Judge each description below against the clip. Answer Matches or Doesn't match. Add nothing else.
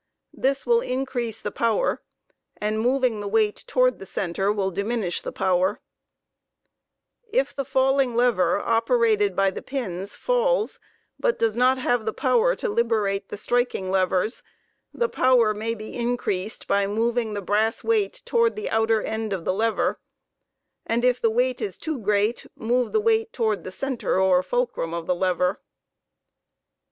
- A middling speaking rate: Matches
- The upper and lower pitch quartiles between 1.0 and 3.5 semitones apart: Doesn't match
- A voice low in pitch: Doesn't match